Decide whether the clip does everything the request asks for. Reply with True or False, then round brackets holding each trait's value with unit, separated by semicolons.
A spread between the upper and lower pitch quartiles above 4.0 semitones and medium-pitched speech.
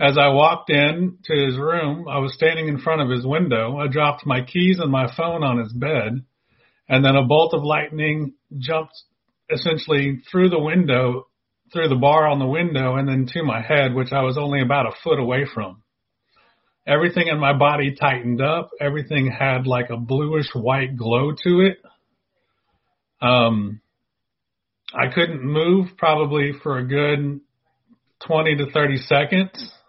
False (3.4 semitones; 145 Hz)